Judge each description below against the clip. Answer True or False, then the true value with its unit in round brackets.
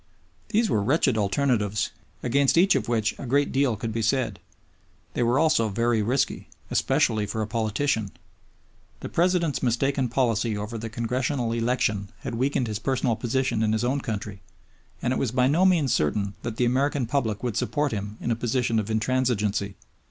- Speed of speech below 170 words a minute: False (175 wpm)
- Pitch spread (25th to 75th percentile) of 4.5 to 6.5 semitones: False (3.6 semitones)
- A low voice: True (120 Hz)